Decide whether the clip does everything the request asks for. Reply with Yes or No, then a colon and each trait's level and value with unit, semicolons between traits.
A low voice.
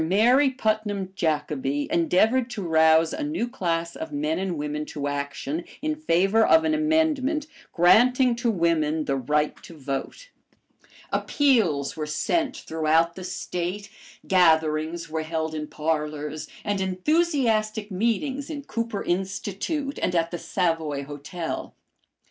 No: medium, 180 Hz